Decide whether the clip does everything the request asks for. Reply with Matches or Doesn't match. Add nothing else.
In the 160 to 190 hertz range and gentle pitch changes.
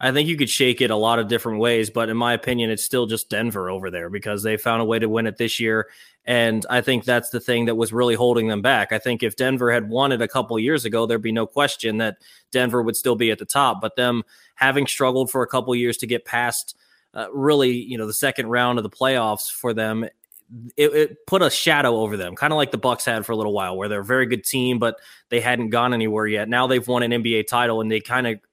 Doesn't match